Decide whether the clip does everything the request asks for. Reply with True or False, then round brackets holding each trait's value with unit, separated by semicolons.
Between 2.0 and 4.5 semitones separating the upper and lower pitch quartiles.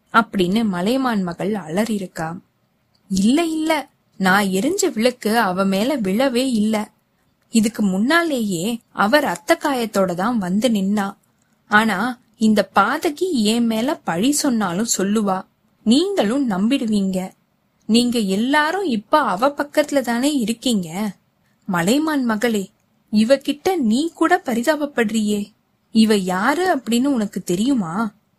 False (5.2 semitones)